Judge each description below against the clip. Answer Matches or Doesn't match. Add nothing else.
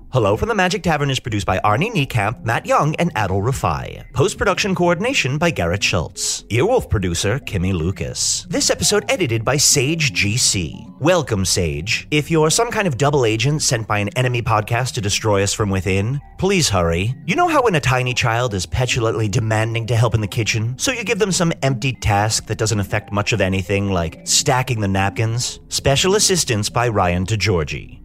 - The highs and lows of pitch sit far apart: Matches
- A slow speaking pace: Doesn't match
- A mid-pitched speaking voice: Doesn't match